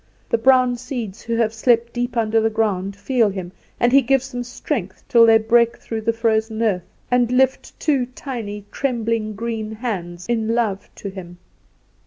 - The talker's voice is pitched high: Yes, high, 230 Hz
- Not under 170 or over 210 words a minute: Yes, average, 175 wpm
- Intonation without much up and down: Yes, narrow, 2.3 semitones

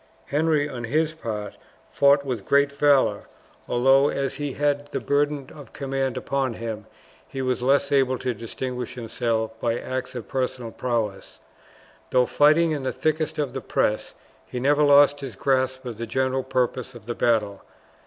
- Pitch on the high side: No, low, 130 Hz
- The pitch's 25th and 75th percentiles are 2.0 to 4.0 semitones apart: Yes, average, 3.1 semitones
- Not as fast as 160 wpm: No, average, 165 wpm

